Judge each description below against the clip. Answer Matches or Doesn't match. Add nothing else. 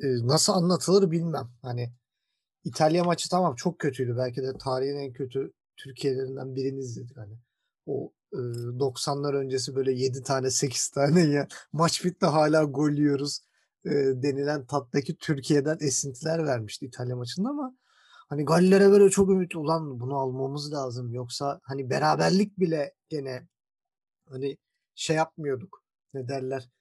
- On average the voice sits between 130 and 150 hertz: Matches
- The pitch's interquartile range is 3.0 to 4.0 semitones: Matches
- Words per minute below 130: Doesn't match